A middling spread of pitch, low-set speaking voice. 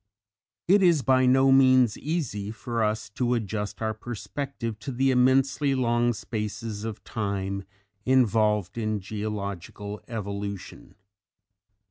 Yes: average, 3.8 semitones; low, 115 Hz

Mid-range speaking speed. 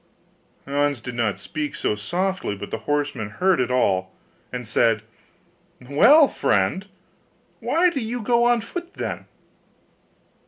No: slow, 130 wpm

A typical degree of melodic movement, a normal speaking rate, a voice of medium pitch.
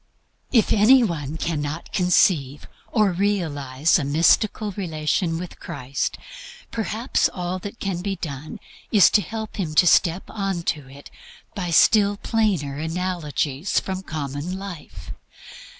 No: average, 4.9 semitones; slow, 130 wpm; medium, 175 Hz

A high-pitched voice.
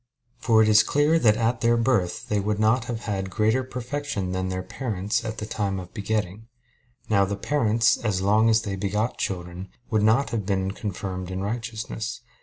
No: low, 105 Hz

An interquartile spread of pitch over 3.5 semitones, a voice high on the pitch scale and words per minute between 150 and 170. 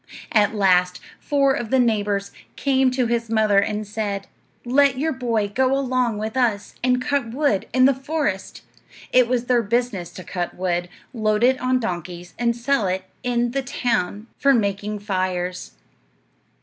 Yes: average, 4.2 semitones; high, 230 Hz; average, 160 wpm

